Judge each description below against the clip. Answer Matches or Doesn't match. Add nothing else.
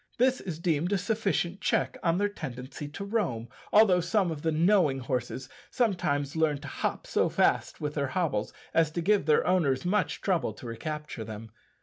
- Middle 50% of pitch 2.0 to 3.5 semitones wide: Doesn't match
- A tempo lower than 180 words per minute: Doesn't match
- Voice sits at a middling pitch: Matches